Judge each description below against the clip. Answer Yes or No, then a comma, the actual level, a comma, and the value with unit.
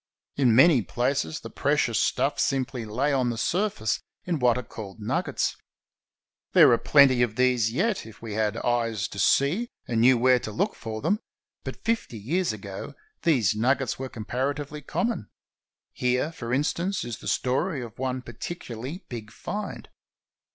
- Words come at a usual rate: Yes, average, 160 wpm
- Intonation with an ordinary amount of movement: Yes, average, 4.4 semitones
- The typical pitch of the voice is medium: No, low, 125 Hz